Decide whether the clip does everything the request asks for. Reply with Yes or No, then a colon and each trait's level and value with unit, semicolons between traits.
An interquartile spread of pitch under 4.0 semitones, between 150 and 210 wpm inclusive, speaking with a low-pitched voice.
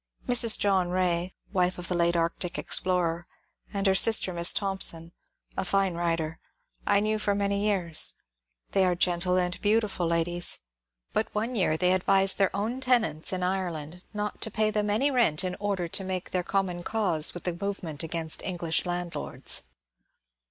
No: average, 2.8 semitones; average, 165 wpm; medium, 185 Hz